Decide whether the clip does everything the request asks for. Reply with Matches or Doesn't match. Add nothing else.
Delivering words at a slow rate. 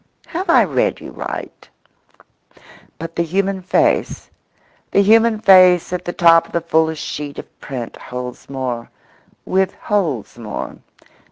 Matches